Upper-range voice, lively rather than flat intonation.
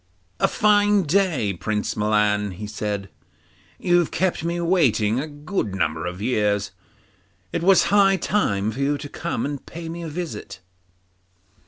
No: medium, 145 Hz; wide, 8.9 semitones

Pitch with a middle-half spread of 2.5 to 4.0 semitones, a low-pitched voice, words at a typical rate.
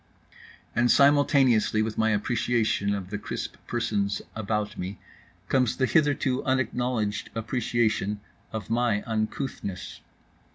No: average, 3.3 semitones; low, 110 Hz; slow, 110 wpm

